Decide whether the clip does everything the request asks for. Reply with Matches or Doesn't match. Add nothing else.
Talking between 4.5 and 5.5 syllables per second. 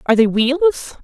Matches